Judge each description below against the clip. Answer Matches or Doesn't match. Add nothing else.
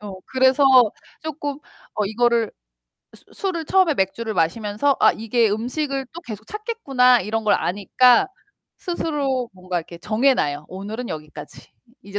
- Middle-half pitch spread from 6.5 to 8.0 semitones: Doesn't match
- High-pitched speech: Matches